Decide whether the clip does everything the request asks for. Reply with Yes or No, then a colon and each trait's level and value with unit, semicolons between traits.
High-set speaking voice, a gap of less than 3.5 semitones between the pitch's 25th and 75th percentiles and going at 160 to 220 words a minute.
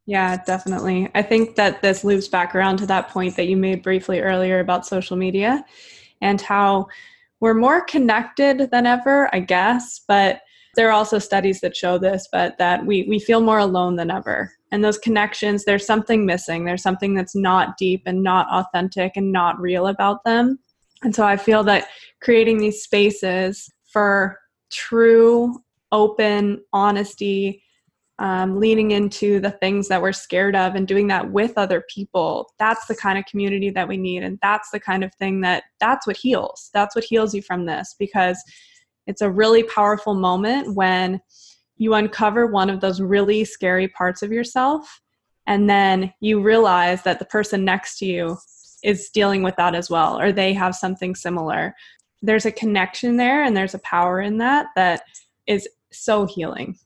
Yes: high, 200 Hz; narrow, 2.6 semitones; average, 175 wpm